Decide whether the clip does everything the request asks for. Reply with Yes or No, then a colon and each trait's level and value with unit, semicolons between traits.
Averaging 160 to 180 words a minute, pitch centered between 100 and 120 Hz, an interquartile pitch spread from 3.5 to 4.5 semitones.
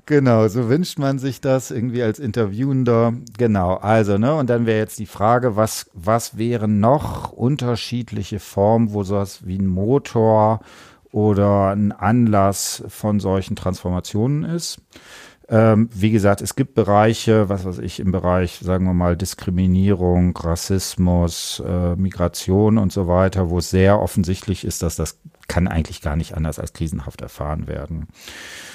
No: average, 150 wpm; low, 105 Hz; average, 3.8 semitones